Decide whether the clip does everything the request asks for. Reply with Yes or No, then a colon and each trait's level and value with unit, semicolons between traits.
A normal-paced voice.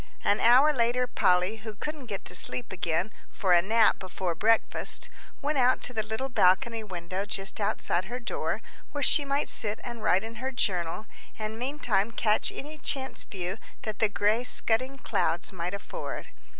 Yes: average, 175 wpm